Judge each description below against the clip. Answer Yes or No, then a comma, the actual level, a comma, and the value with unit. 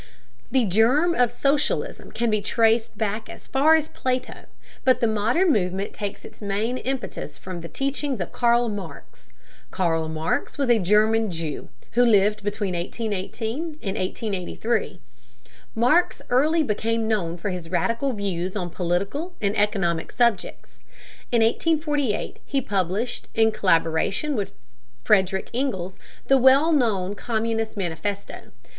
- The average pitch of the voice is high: Yes, high, 220 Hz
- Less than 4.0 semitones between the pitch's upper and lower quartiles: No, average, 4.7 semitones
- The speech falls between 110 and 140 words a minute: Yes, slow, 135 wpm